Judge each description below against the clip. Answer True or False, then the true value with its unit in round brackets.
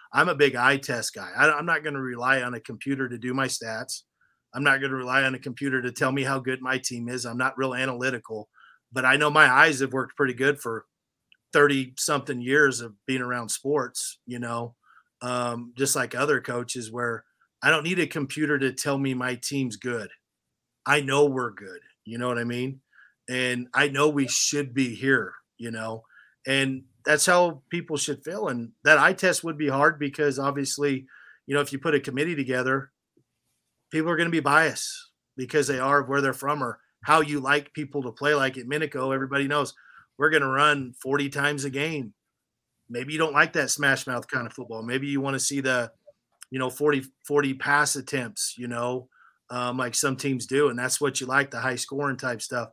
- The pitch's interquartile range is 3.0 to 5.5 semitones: False (2.4 semitones)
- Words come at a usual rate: False (215 wpm)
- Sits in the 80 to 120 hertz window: False (135 Hz)